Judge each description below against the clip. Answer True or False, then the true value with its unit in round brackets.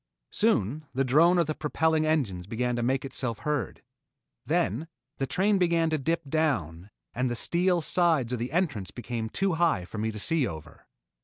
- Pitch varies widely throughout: True (6.0 semitones)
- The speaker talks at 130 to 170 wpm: False (180 wpm)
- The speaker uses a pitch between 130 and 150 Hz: True (140 Hz)